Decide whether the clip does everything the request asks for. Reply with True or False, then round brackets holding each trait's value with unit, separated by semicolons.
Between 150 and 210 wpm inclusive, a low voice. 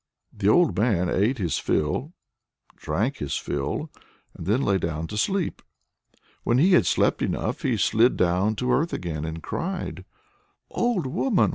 True (155 wpm; 110 Hz)